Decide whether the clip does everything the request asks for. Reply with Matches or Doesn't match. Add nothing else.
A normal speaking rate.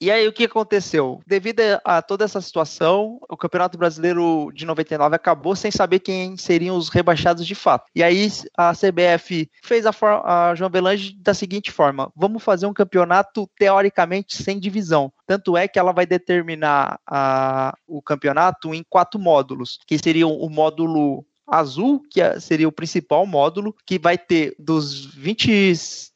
Matches